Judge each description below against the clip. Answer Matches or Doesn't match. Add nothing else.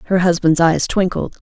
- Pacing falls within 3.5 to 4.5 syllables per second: Doesn't match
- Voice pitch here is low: Doesn't match